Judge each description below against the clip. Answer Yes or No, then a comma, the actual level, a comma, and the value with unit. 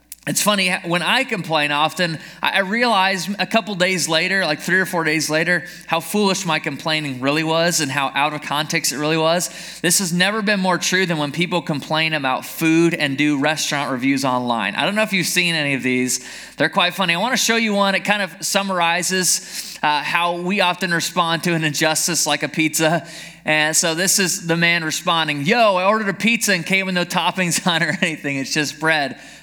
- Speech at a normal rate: No, fast, 215 wpm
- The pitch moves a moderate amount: Yes, average, 3.3 semitones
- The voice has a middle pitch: Yes, medium, 170 Hz